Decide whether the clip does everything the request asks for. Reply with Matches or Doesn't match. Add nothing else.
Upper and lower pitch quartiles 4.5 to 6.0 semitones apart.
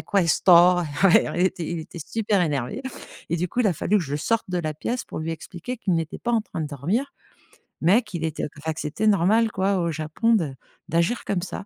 Matches